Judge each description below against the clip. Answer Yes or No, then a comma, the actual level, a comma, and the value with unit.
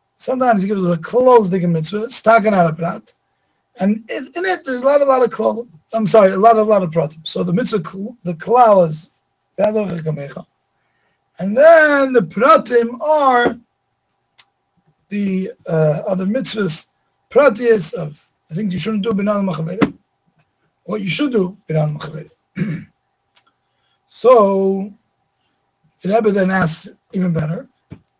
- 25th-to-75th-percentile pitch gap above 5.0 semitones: Yes, wide, 5.5 semitones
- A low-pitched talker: No, high, 205 Hz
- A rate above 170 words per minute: No, slow, 135 wpm